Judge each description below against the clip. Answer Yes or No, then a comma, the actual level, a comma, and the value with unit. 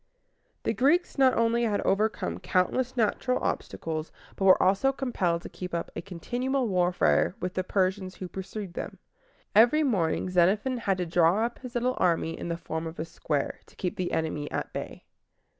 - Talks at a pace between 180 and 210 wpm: Yes, average, 185 wpm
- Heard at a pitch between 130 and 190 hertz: Yes, medium, 185 Hz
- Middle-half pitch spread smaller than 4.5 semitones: No, wide, 5.6 semitones